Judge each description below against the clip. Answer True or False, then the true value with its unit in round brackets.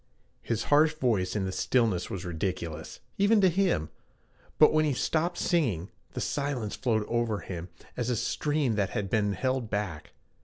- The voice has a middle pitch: False (115 Hz)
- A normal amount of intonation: False (7.2 semitones)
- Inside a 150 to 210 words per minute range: True (165 wpm)